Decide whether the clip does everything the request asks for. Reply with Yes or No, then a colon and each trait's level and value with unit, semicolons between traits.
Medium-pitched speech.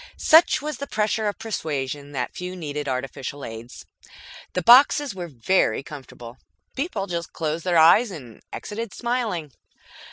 Yes: medium, 170 Hz